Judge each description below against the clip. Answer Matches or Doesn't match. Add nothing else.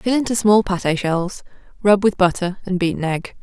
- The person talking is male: Doesn't match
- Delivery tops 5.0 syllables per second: Doesn't match